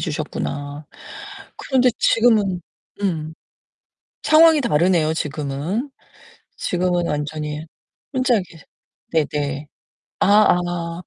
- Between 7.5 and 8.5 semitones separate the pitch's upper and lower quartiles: No, average, 5.2 semitones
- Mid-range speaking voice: Yes, medium, 165 Hz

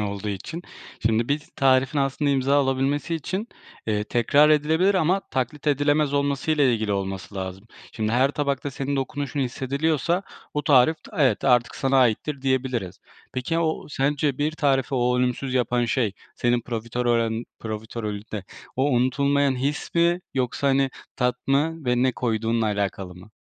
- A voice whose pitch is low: Yes, low, 130 Hz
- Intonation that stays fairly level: No, average, 3.7 semitones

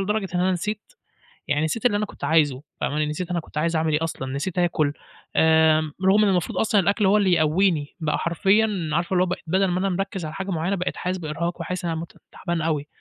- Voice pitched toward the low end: No, medium, 175 Hz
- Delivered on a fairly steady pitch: No, average, 3.5 semitones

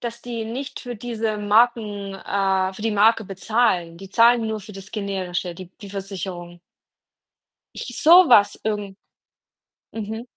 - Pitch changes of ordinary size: Yes, average, 3.0 semitones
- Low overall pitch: No, high, 210 Hz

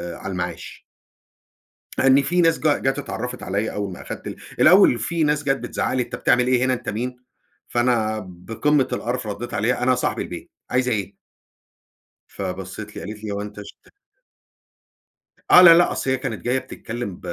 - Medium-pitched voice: No, low, 120 Hz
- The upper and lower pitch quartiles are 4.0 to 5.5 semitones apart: Yes, average, 4.3 semitones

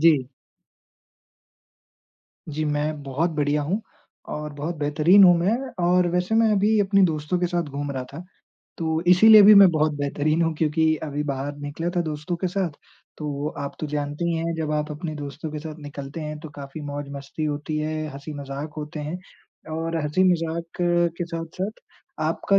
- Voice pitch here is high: No, medium, 155 Hz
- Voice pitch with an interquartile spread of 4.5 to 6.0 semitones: No, average, 2.8 semitones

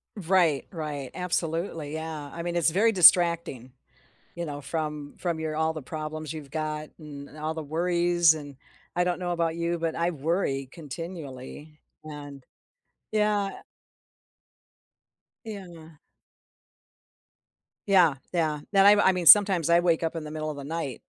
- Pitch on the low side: No, medium, 160 Hz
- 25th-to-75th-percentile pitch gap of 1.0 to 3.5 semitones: Yes, narrow, 2.5 semitones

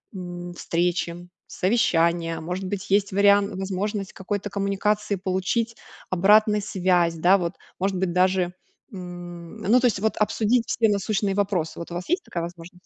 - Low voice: No, high, 190 Hz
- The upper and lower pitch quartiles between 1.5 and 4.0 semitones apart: Yes, average, 2.7 semitones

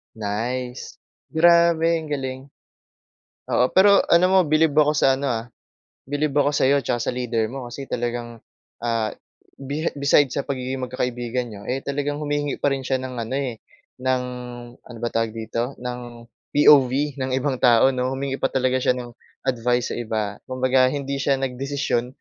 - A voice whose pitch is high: No, low, 130 Hz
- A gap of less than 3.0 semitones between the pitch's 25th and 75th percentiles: Yes, narrow, 2.6 semitones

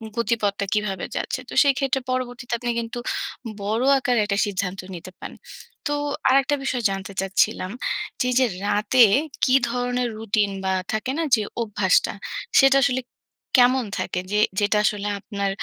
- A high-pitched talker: Yes, high, 225 Hz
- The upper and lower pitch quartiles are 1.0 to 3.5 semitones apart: No, average, 3.9 semitones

